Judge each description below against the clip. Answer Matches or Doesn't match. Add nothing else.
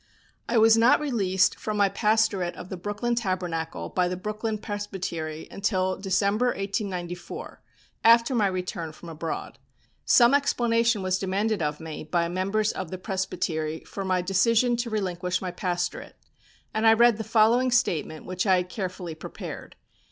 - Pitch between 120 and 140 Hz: Doesn't match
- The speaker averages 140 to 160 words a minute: Matches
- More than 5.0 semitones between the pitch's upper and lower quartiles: Doesn't match